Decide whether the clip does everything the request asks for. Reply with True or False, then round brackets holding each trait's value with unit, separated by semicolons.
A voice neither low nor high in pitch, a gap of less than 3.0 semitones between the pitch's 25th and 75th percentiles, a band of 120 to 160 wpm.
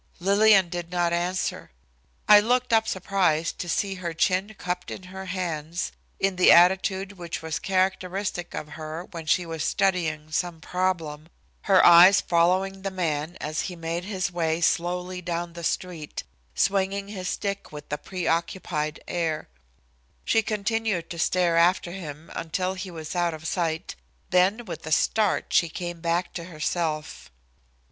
True (175 Hz; 2.4 semitones; 155 wpm)